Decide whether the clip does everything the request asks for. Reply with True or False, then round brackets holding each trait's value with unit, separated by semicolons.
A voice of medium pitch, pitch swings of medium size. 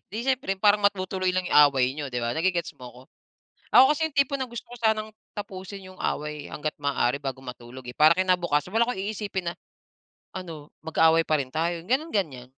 False (180 Hz; 6.1 semitones)